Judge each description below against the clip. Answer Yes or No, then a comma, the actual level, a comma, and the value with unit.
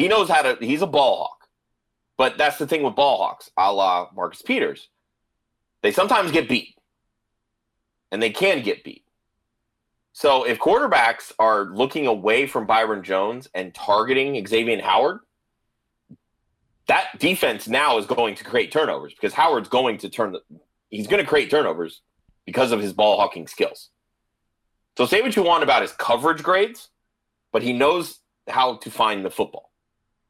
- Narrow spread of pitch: Yes, narrow, 1.9 semitones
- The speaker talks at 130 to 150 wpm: No, average, 165 wpm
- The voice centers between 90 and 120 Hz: Yes, low, 115 Hz